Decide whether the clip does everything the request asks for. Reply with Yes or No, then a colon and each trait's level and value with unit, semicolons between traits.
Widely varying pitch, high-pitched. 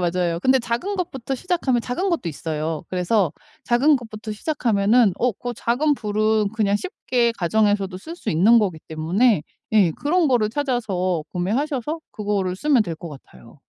Yes: wide, 5.9 semitones; high, 220 Hz